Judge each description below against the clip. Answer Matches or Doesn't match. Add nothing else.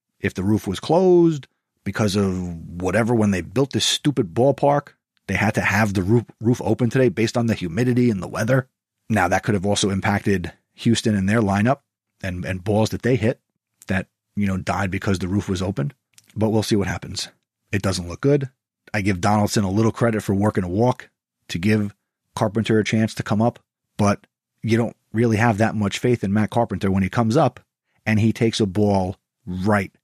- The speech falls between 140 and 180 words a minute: Doesn't match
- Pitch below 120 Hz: Matches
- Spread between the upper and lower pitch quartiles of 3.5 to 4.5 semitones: Doesn't match